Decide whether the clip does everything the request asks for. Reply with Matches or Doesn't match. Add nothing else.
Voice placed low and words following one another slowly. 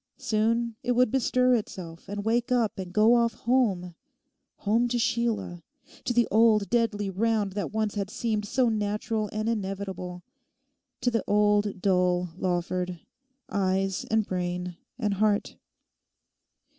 Doesn't match